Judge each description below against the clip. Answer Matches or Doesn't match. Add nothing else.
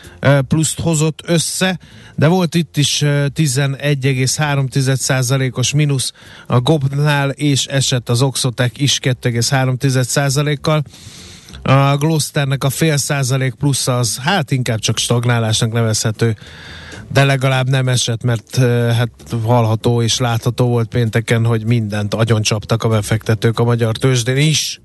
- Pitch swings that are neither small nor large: Matches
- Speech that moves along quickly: Doesn't match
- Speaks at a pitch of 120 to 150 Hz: Matches